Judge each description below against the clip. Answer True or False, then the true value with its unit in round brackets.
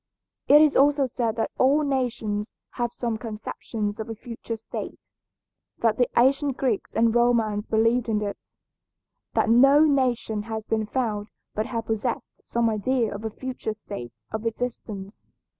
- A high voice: True (230 Hz)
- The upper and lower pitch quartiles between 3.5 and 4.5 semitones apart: False (2.6 semitones)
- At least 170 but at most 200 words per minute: False (155 wpm)